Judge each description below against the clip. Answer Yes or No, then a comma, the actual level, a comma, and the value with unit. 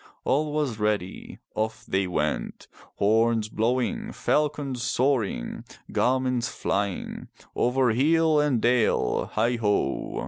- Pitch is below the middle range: Yes, low, 120 Hz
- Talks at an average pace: No, slow, 100 wpm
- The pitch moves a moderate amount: Yes, average, 4.3 semitones